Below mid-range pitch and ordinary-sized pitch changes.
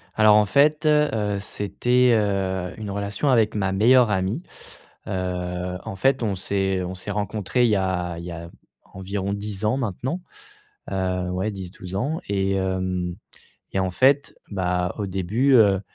Yes: low, 100 Hz; average, 3.0 semitones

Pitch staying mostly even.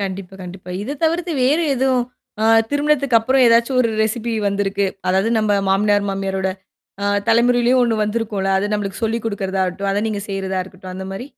No: average, 3.8 semitones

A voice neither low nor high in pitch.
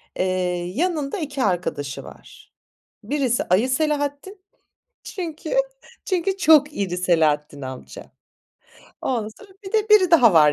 No: very high, 265 Hz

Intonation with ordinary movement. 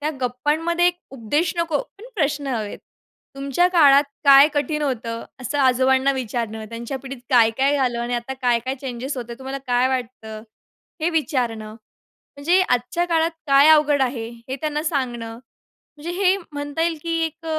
Yes: average, 3.7 semitones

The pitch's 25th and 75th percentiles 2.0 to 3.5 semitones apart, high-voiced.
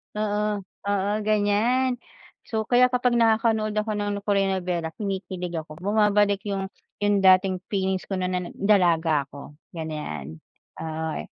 Yes: average, 3.1 semitones; high, 200 Hz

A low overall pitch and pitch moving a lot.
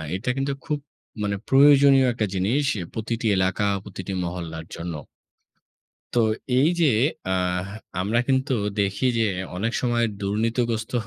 Yes: low, 110 Hz; wide, 5.7 semitones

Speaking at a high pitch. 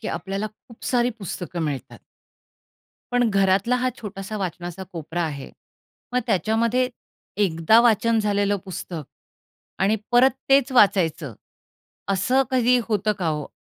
Yes: high, 205 Hz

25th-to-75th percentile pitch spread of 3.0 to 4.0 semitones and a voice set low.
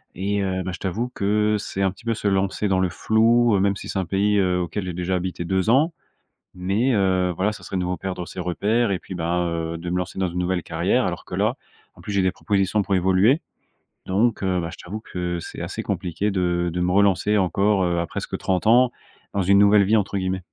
No: narrow, 2.4 semitones; very low, 95 Hz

